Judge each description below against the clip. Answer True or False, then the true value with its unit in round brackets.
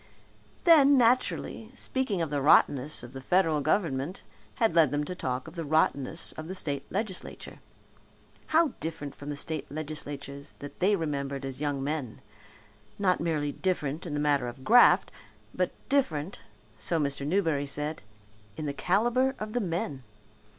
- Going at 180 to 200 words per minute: False (155 wpm)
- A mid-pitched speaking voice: True (155 Hz)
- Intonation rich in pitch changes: False (4.8 semitones)